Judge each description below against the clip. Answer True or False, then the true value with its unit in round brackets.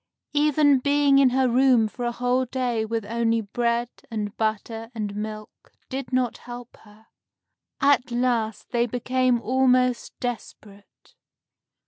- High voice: True (240 Hz)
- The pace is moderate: False (130 wpm)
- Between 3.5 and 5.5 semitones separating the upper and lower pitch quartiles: False (2.4 semitones)